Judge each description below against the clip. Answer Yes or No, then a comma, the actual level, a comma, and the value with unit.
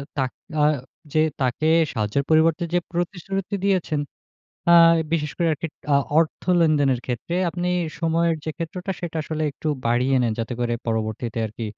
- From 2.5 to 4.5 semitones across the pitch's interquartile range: No, wide, 5.4 semitones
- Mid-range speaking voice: Yes, medium, 155 Hz